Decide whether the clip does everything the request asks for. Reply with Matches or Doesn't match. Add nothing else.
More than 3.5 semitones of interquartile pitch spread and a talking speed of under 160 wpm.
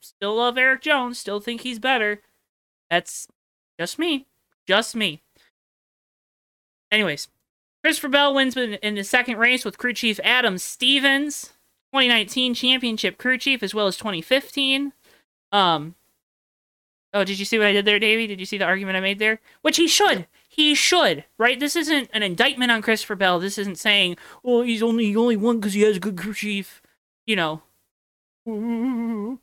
Doesn't match